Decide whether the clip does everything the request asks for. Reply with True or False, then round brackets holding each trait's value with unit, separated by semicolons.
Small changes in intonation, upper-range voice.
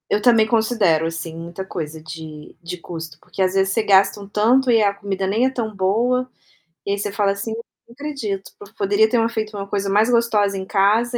False (3.1 semitones; 200 Hz)